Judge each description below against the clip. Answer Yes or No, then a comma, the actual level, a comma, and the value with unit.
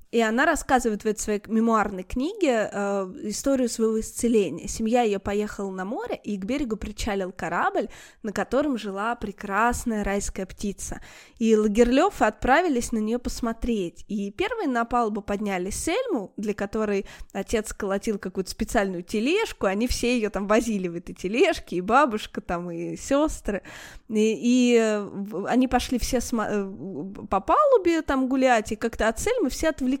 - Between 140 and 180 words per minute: Yes, average, 150 wpm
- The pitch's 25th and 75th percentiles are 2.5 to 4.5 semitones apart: Yes, average, 3.5 semitones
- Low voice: No, high, 225 Hz